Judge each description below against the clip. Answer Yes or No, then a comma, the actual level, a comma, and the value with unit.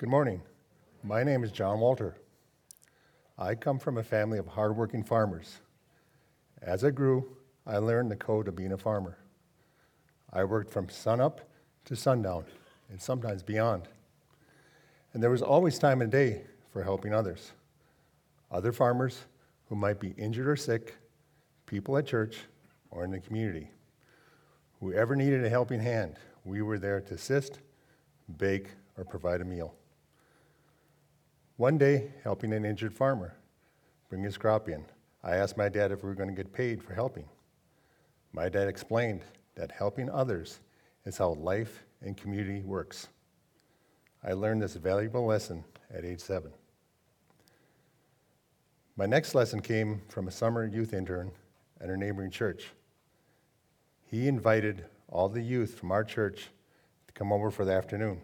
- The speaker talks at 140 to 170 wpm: Yes, average, 150 wpm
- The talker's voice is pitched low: Yes, low, 110 Hz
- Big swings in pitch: No, average, 4.3 semitones